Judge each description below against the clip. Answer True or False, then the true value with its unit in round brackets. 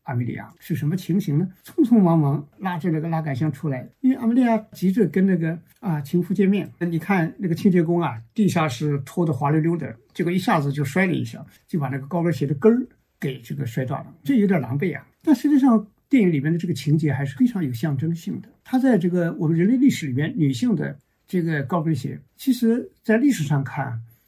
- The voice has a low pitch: False (170 Hz)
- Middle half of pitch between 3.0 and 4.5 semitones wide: False (5.3 semitones)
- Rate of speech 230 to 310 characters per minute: False (340 characters per minute)